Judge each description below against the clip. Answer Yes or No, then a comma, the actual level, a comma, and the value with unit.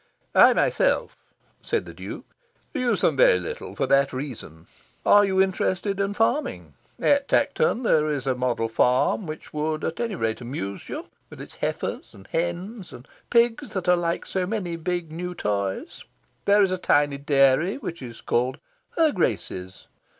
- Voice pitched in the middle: Yes, medium, 170 Hz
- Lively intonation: Yes, wide, 7.2 semitones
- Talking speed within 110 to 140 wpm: No, average, 165 wpm